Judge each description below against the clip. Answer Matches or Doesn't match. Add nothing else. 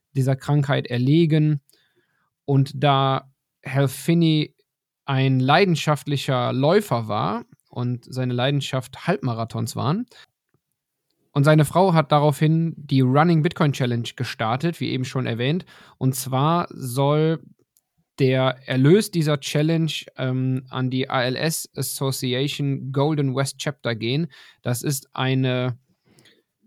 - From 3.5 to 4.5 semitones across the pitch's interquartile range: Doesn't match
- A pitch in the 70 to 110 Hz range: Doesn't match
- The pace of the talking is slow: Matches